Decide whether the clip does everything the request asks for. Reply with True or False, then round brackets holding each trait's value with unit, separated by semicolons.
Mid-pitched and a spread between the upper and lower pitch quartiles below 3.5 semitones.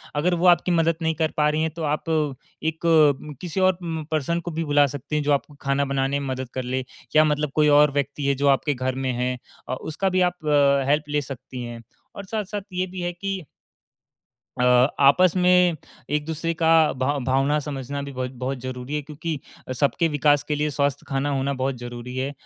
True (145 Hz; 3.0 semitones)